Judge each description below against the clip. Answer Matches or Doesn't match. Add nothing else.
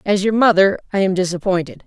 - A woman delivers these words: Matches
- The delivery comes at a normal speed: Matches